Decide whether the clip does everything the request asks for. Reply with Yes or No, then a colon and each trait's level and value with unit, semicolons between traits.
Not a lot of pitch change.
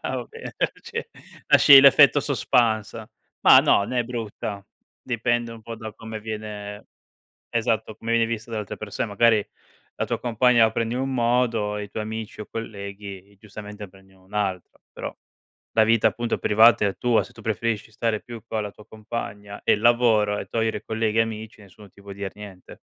Yes: narrow, 2.1 semitones